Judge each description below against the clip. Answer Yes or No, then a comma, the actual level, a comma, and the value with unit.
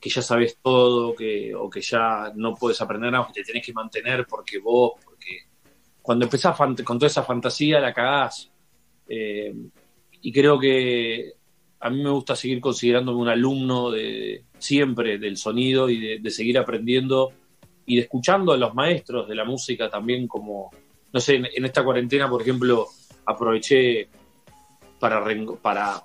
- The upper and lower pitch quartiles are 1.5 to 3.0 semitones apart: Yes, narrow, 2.5 semitones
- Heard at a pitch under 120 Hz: No, low, 125 Hz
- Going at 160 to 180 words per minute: Yes, fast, 170 wpm